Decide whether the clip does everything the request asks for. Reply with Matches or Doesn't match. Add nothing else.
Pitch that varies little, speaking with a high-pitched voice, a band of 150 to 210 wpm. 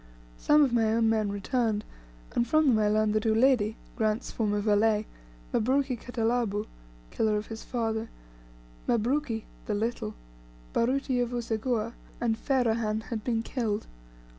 Doesn't match